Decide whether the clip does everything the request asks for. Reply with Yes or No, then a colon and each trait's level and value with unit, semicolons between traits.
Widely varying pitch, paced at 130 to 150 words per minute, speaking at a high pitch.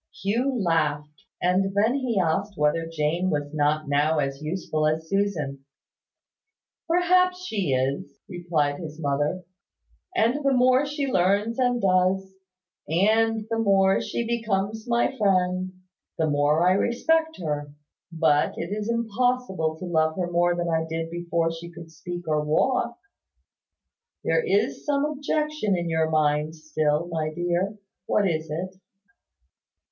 No: wide, 6.0 semitones; average, 140 wpm; medium, 180 Hz